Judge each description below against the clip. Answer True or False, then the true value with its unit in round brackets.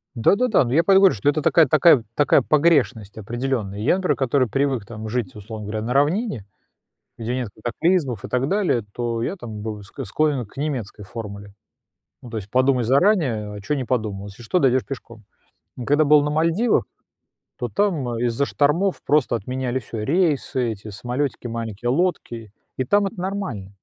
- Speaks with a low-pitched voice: True (125 Hz)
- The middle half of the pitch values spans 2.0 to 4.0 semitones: False (5.2 semitones)